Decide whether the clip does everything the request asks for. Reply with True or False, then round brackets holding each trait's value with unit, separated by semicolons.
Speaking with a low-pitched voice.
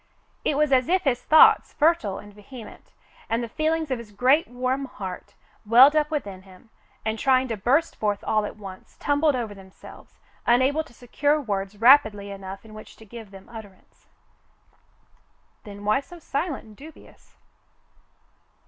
False (235 Hz)